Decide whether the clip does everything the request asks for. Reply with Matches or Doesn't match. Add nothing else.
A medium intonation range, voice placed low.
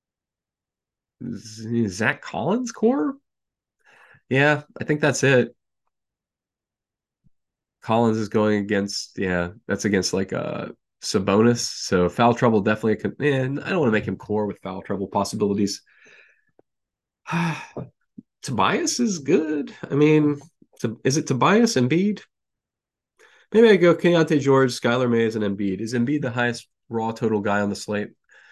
Doesn't match